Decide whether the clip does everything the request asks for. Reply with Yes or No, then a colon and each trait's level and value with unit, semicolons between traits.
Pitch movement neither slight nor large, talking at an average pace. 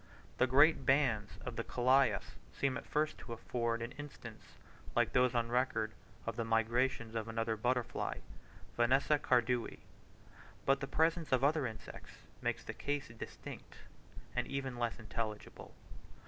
Yes: average, 3.0 semitones; average, 145 wpm